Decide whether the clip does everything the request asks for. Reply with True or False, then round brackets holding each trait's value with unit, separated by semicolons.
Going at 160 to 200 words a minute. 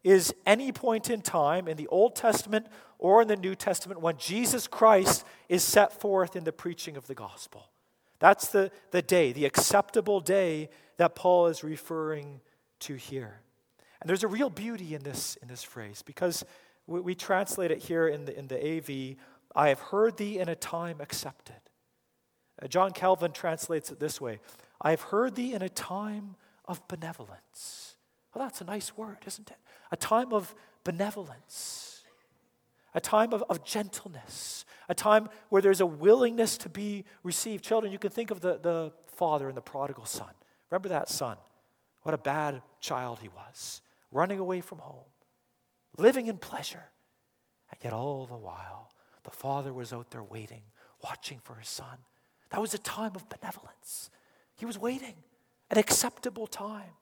True (175 wpm)